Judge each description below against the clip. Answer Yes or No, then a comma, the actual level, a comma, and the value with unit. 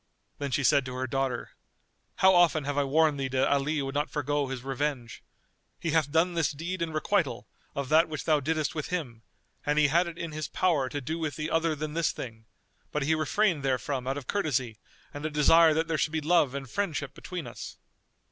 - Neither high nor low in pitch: Yes, medium, 150 Hz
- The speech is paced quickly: Yes, fast, 220 wpm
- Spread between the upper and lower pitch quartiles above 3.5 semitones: No, average, 3.0 semitones